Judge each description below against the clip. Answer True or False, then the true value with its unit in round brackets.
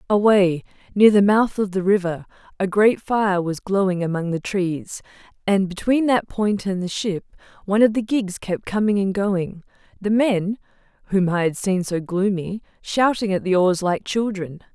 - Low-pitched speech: False (195 Hz)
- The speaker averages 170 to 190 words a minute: True (180 wpm)